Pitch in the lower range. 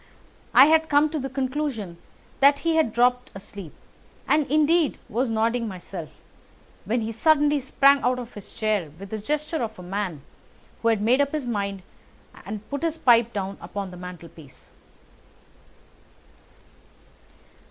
No: high, 235 Hz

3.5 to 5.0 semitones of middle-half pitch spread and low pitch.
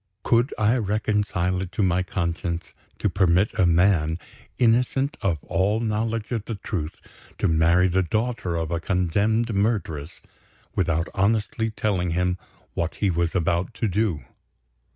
Yes: average, 4.1 semitones; very low, 95 Hz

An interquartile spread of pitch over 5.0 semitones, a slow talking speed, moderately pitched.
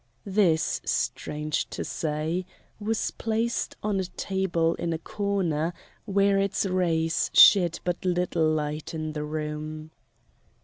No: average, 3.8 semitones; slow, 125 wpm; medium, 170 Hz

